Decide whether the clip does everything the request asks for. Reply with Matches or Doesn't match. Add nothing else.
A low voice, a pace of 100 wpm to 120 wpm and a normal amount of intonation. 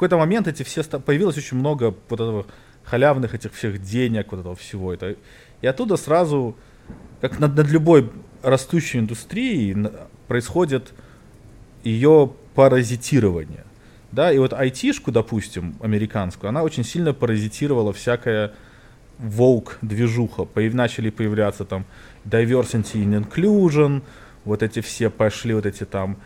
Doesn't match